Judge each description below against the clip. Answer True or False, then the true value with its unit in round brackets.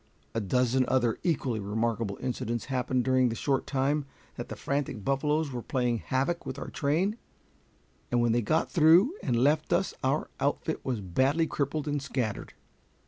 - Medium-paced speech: True (165 wpm)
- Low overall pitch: True (130 Hz)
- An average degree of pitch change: True (3.7 semitones)